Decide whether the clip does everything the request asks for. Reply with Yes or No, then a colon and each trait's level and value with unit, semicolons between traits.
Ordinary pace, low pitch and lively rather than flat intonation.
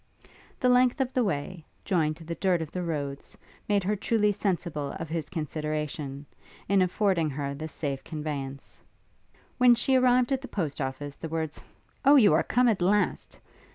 No: average, 175 wpm; medium, 170 Hz; wide, 5.7 semitones